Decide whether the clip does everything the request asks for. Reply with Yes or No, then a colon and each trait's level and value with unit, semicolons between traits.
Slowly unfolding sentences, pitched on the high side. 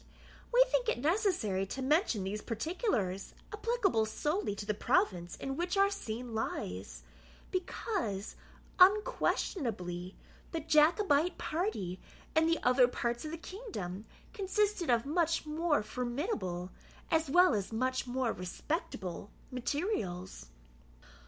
Yes: slow, 120 wpm; very high, 270 Hz